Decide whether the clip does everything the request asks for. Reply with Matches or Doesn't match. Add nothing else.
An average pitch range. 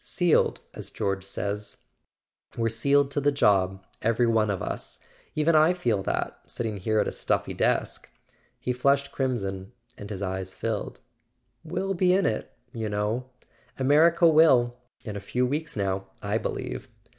Doesn't match